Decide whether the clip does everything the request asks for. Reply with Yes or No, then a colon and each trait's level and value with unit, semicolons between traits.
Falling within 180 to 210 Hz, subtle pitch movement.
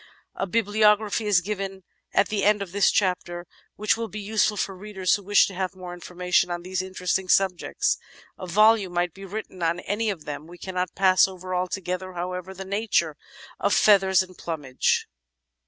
Yes: high, 190 Hz; narrow, 2.2 semitones